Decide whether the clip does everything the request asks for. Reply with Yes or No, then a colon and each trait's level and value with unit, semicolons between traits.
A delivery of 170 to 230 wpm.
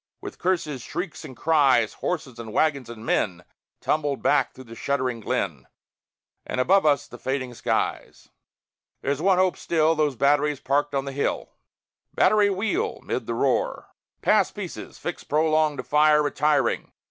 No: average, 155 wpm